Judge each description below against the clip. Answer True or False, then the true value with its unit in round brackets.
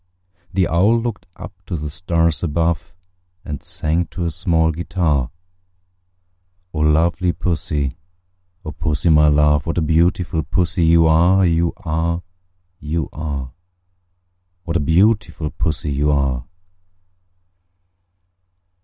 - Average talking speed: False (120 wpm)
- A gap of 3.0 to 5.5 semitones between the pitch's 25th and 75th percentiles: False (2.4 semitones)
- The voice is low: True (80 Hz)